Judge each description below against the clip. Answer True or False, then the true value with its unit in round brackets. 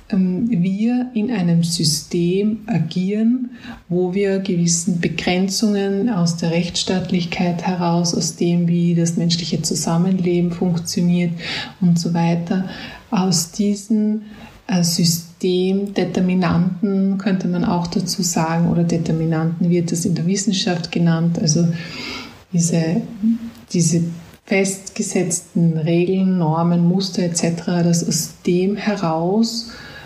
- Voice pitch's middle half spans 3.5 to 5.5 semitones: False (2.7 semitones)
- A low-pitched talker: False (180 Hz)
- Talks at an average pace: False (100 wpm)